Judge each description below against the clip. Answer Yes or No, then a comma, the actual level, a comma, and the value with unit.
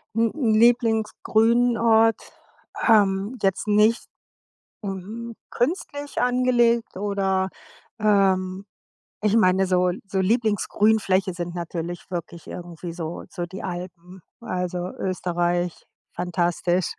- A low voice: No, high, 195 Hz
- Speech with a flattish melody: No, average, 4.0 semitones